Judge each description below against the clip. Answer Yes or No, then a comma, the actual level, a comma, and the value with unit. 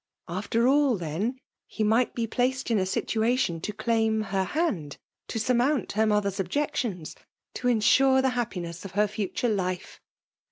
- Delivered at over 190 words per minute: No, average, 165 wpm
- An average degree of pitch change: Yes, average, 4.4 semitones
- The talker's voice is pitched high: Yes, high, 220 Hz